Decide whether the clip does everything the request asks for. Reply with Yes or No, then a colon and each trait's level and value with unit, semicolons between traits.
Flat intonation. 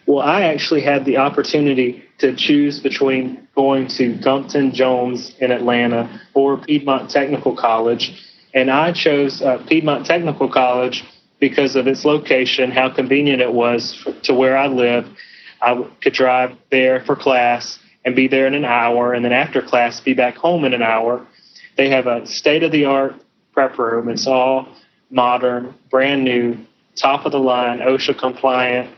Yes: narrow, 1.8 semitones